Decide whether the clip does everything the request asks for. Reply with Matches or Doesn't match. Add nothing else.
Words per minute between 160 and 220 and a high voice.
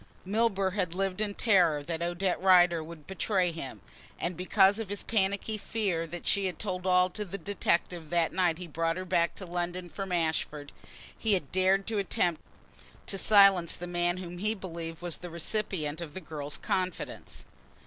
Doesn't match